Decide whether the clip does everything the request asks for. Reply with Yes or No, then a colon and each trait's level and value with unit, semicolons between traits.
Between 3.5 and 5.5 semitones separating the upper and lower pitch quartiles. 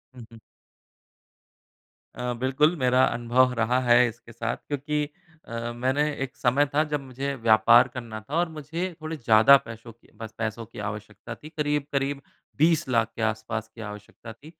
Yes: average, 4.0 semitones